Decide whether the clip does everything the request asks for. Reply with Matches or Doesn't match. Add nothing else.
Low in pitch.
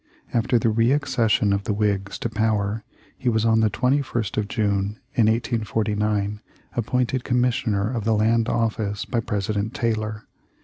Matches